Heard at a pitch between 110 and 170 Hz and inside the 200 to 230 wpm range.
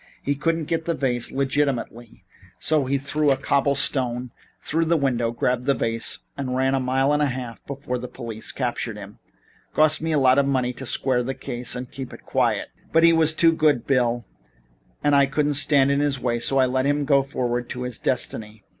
Yes: low, 135 Hz; fast, 205 wpm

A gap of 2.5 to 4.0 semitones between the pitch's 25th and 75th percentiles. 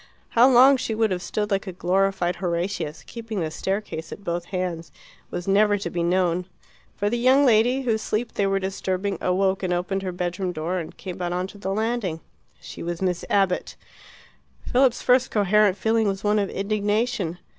Yes: average, 3.2 semitones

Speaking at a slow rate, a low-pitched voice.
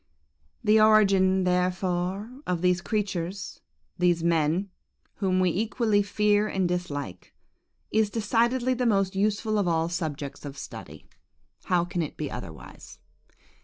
No: slow, 120 wpm; medium, 185 Hz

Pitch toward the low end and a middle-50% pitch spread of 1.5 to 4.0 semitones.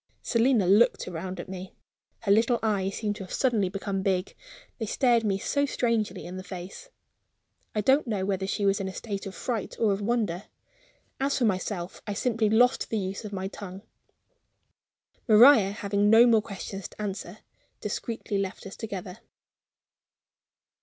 No: high, 205 Hz; average, 2.9 semitones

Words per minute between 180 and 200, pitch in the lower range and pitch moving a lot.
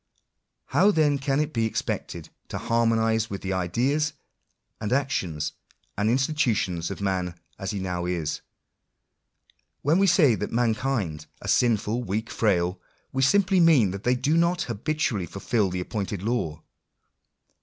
No: average, 145 wpm; low, 115 Hz; wide, 6.4 semitones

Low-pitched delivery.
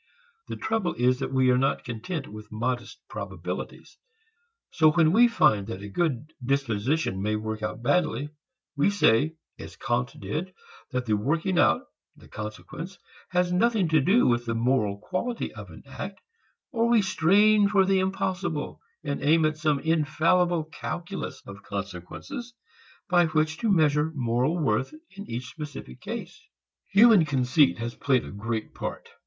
No: medium, 150 Hz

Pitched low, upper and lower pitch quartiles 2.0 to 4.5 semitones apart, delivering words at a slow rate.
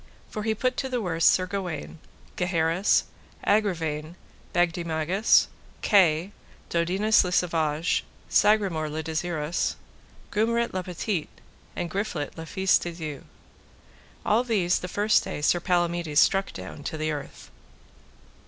No: medium, 175 Hz; average, 4.0 semitones; slow, 125 wpm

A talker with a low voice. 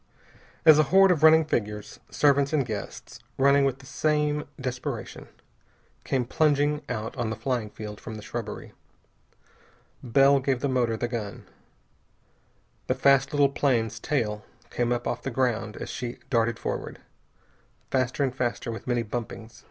Yes: low, 125 Hz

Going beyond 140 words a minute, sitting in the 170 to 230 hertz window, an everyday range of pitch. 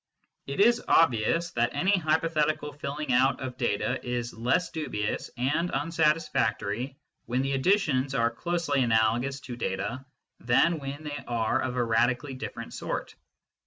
No: average, 150 wpm; low, 135 Hz; average, 4.4 semitones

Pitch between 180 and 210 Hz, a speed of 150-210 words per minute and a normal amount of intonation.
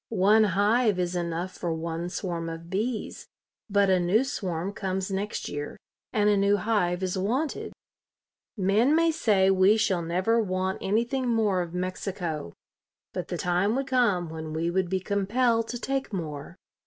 Yes: high, 190 Hz; average, 165 wpm; average, 3.7 semitones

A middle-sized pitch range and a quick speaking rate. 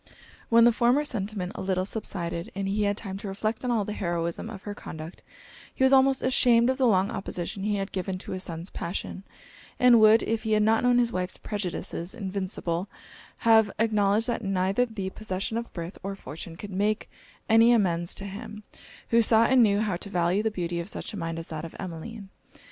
Yes: average, 3.5 semitones; fast, 210 wpm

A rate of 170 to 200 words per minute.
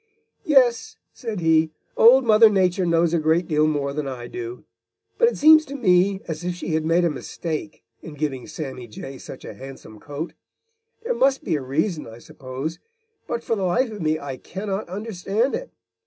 Yes: average, 190 wpm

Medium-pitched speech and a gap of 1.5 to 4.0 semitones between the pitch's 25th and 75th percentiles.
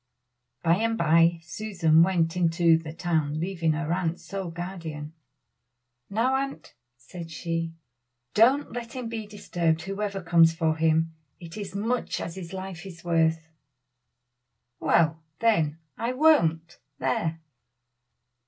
Yes: medium, 170 Hz; average, 3.4 semitones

